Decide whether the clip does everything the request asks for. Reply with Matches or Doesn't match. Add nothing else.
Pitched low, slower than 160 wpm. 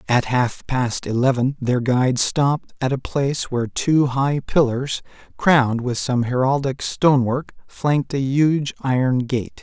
Matches